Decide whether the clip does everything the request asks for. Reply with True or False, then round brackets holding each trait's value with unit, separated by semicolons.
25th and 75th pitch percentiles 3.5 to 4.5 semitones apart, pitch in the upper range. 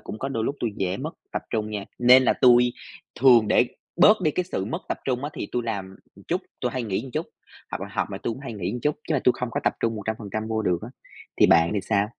False (3.9 semitones; 115 Hz)